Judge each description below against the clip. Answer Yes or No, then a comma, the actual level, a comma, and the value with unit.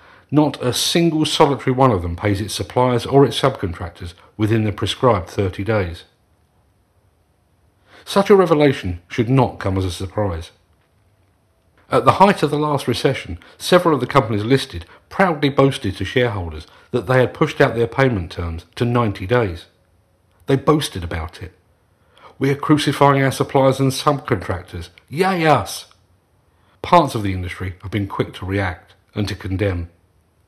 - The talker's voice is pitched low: Yes, low, 105 Hz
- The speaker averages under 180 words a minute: Yes, average, 155 wpm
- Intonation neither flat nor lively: No, wide, 6.6 semitones